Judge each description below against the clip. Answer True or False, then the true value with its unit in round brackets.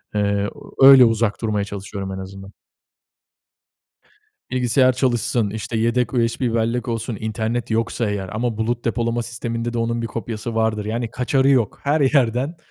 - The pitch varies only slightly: True (2.1 semitones)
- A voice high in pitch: False (115 Hz)